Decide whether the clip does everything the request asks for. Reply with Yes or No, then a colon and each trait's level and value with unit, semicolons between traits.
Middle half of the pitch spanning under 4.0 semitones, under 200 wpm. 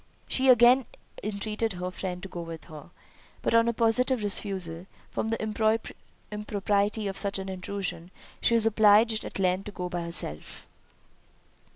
Yes: average, 3.4 semitones; average, 155 wpm